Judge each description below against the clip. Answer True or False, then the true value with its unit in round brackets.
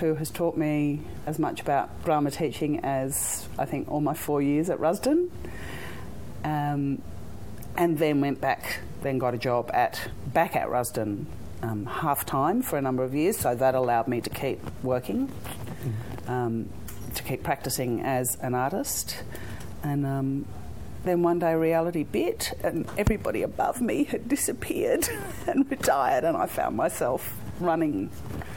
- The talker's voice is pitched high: False (135 Hz)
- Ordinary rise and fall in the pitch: True (4.6 semitones)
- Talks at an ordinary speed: True (155 wpm)